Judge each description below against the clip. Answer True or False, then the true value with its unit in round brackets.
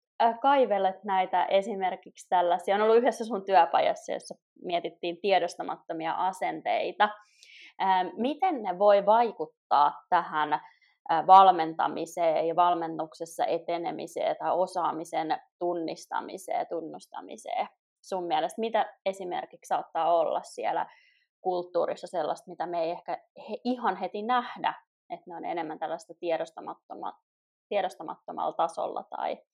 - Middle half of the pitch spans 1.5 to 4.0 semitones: False (5.2 semitones)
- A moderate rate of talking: True (105 wpm)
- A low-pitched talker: False (190 Hz)